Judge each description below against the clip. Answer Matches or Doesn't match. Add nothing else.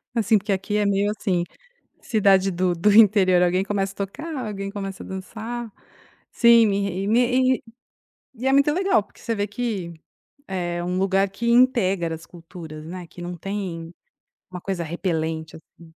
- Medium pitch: Doesn't match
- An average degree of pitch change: Matches